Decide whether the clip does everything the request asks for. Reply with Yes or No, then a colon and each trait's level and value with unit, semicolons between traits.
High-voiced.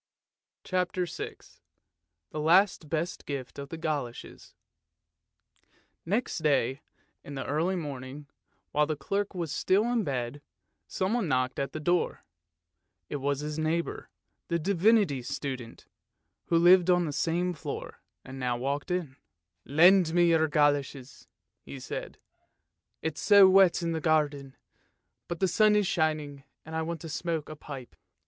No: medium, 155 Hz